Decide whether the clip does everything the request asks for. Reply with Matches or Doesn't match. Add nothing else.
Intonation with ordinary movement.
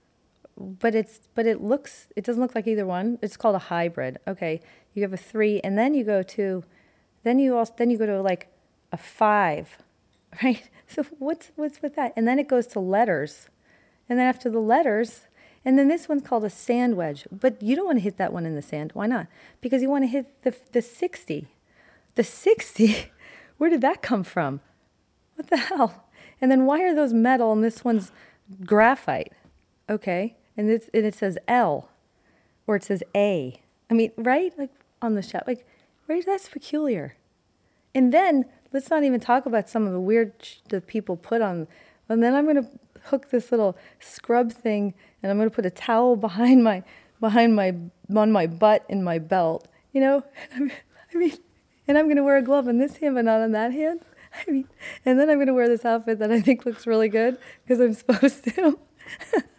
Matches